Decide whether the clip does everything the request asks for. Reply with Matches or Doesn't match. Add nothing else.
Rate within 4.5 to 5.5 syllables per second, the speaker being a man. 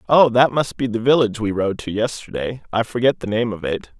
Doesn't match